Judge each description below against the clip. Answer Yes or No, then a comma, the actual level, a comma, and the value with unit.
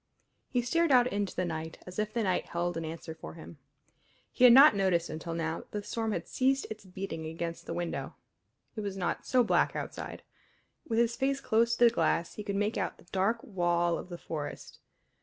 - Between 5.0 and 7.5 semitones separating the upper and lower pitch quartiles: Yes, wide, 5.5 semitones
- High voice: Yes, high, 195 Hz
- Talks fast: Yes, fast, 215 wpm